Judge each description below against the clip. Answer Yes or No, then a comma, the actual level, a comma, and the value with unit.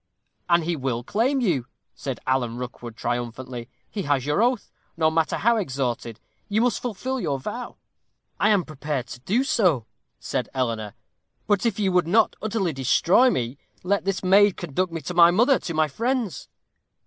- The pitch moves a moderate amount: No, wide, 8.2 semitones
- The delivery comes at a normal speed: Yes, average, 170 wpm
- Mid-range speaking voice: Yes, medium, 170 Hz